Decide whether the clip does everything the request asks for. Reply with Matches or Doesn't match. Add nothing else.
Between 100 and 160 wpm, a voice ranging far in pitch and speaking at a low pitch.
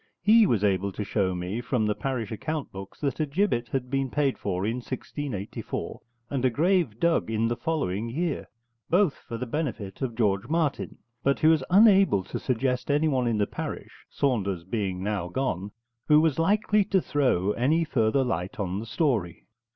Doesn't match